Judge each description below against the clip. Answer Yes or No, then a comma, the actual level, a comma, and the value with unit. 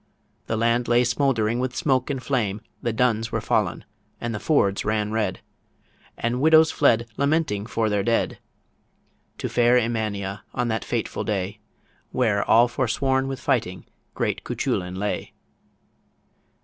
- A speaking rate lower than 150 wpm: Yes, average, 140 wpm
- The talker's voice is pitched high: No, low, 115 Hz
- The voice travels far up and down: No, average, 3.1 semitones